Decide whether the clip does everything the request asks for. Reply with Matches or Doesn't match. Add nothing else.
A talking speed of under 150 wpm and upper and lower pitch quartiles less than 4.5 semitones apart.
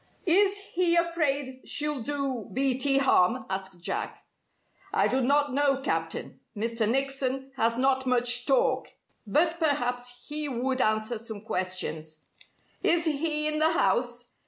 Matches